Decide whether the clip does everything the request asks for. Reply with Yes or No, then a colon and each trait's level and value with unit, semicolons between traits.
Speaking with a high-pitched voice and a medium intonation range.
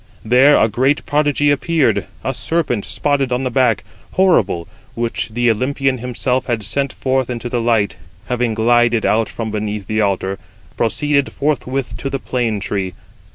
No: low, 125 Hz; average, 3.7 semitones